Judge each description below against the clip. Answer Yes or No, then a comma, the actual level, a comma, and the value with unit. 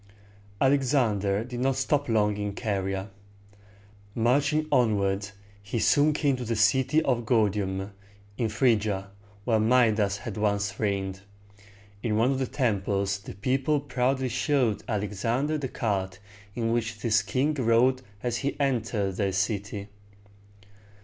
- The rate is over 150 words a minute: No, slow, 135 wpm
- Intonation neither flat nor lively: Yes, average, 4.3 semitones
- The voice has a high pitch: No, low, 115 Hz